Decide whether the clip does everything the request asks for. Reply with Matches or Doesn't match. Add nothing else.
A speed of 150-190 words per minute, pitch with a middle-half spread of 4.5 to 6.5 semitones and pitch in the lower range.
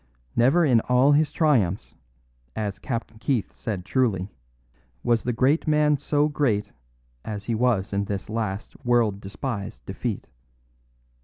Doesn't match